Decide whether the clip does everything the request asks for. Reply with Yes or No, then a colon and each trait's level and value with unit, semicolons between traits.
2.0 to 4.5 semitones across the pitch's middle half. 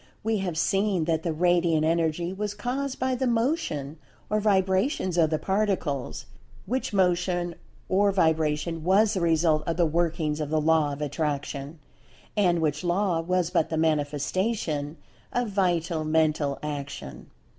Yes: average, 3.9 semitones